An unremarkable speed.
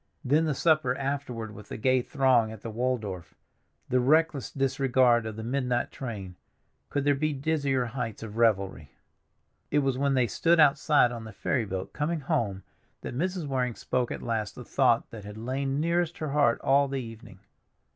Yes: average, 175 wpm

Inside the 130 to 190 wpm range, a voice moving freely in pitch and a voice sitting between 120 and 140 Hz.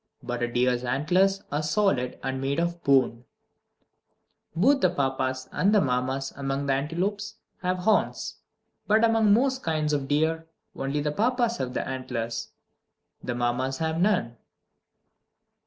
No: average, 140 wpm; wide, 6.8 semitones; medium, 150 Hz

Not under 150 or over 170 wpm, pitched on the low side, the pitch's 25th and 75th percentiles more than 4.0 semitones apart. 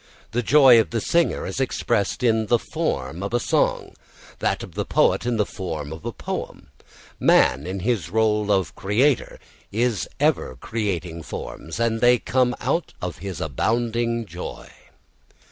Yes: average, 160 wpm; low, 110 Hz; average, 4.8 semitones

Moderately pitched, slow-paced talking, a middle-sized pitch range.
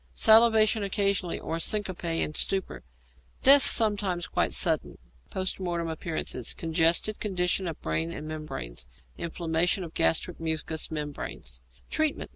Yes: medium, 175 Hz; slow, 120 wpm; average, 3.9 semitones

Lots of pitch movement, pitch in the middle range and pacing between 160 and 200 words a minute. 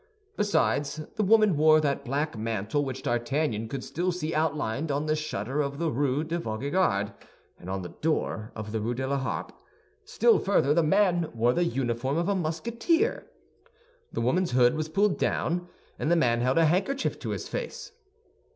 Yes: wide, 6.0 semitones; medium, 150 Hz; average, 180 wpm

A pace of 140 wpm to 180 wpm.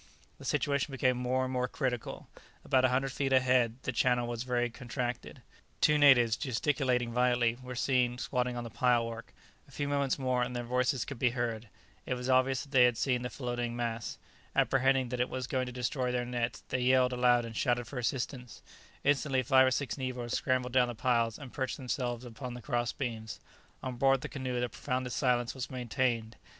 No: average, 200 wpm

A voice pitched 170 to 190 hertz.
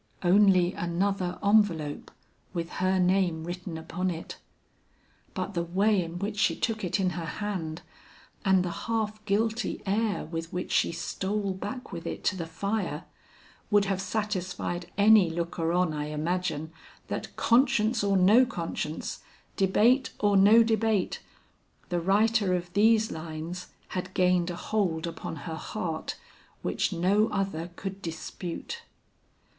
Yes: medium, 185 Hz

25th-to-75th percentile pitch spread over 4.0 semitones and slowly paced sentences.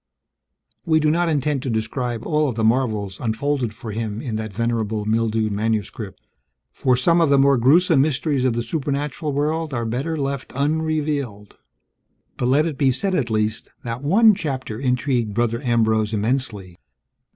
No: average, 4.7 semitones; average, 160 wpm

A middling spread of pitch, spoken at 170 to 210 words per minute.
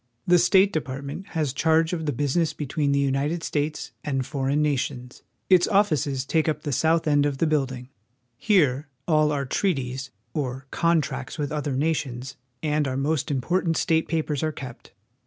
Yes: average, 3.1 semitones; average, 175 wpm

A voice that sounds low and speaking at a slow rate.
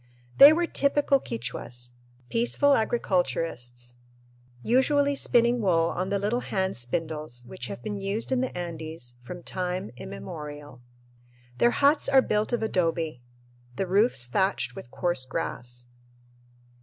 No: medium, 180 Hz; slow, 130 wpm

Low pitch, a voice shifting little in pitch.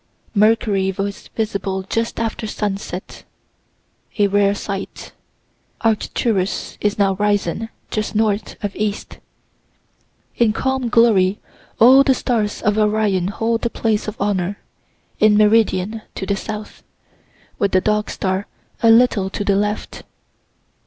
No: high, 210 Hz; narrow, 2.0 semitones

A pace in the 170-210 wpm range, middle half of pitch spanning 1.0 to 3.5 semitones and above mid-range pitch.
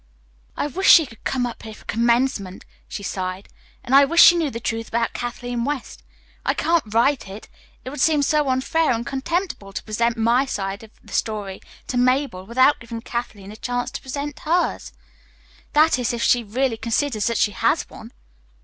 No: average, 190 wpm; average, 4.0 semitones; high, 245 Hz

